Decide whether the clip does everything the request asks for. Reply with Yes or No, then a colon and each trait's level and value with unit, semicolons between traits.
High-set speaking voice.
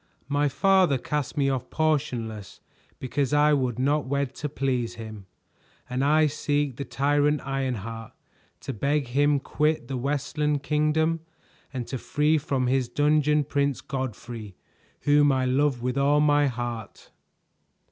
No: medium, 140 Hz